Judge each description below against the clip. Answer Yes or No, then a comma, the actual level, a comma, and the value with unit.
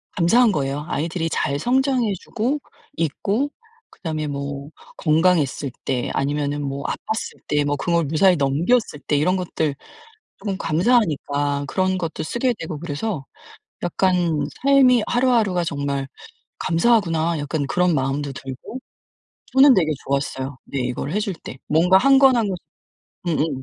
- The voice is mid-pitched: Yes, medium, 165 Hz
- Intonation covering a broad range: Yes, wide, 6.2 semitones